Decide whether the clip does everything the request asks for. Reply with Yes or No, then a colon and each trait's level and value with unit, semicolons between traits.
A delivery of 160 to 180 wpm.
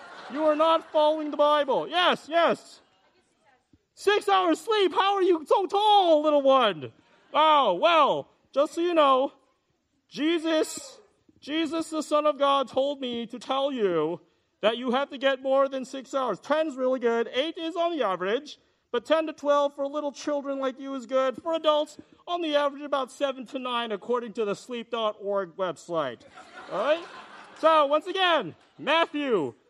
Yes: average, 170 wpm